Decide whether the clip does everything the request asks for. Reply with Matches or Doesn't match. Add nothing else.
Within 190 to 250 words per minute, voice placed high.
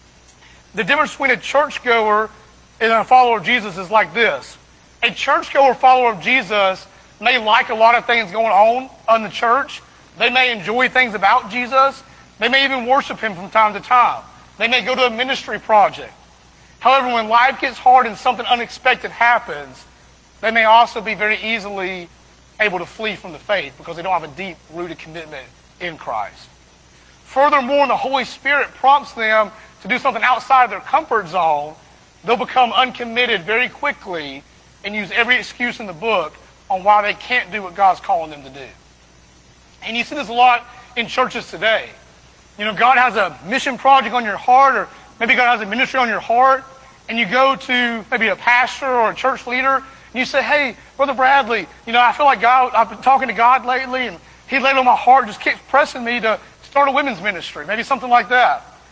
Matches